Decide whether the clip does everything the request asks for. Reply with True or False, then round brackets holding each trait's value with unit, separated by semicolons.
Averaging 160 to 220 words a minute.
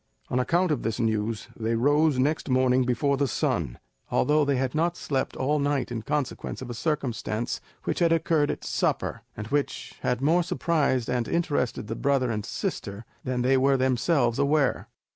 True (180 wpm)